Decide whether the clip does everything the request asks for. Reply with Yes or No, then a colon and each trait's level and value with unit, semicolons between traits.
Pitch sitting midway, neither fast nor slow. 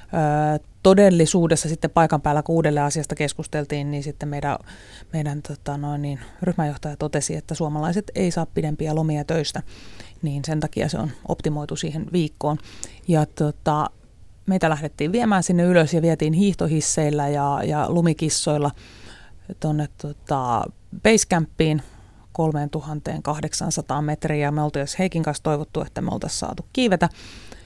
Yes: medium, 155 Hz; average, 130 wpm